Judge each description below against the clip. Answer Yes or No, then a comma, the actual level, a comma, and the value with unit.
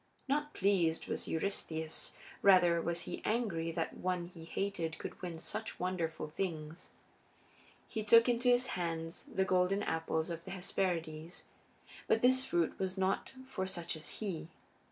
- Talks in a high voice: No, medium, 180 Hz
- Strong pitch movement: No, average, 3.4 semitones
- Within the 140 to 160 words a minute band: Yes, average, 150 wpm